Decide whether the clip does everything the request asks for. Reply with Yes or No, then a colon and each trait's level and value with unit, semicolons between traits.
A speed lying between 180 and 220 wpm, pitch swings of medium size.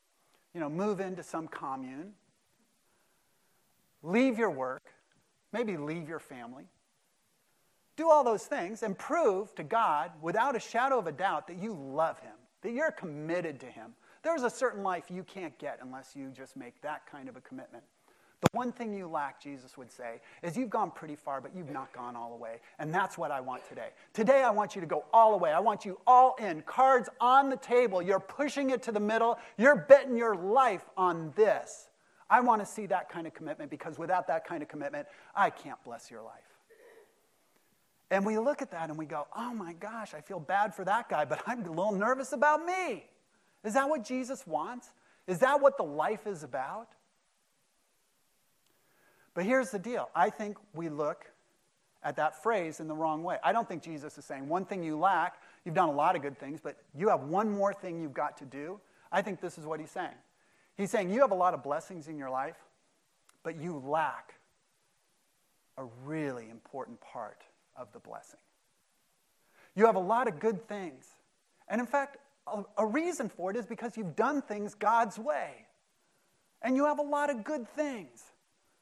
No: average, 200 wpm; wide, 7.3 semitones